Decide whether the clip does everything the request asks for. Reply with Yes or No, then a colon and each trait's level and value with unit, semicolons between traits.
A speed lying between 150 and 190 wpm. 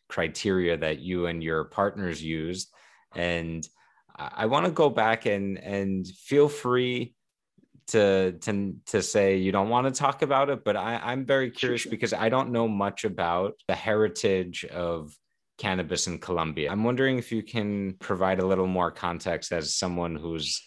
Yes: average, 170 wpm